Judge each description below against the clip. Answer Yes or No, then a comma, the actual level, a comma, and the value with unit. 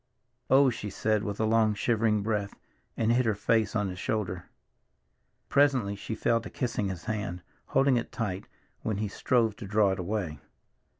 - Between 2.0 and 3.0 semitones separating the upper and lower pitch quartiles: Yes, narrow, 2.5 semitones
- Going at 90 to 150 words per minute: No, average, 175 wpm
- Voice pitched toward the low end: Yes, low, 110 Hz